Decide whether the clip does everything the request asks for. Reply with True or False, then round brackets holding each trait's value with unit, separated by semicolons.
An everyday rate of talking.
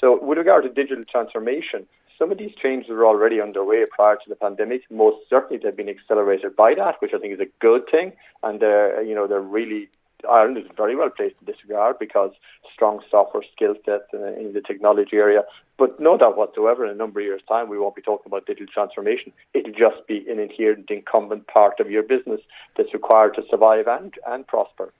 False (210 wpm)